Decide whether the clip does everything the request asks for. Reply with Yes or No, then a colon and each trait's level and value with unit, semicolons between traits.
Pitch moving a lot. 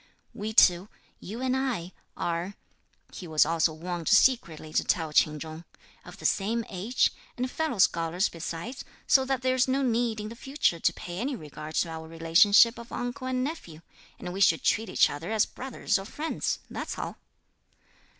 Yes: wide, 7.0 semitones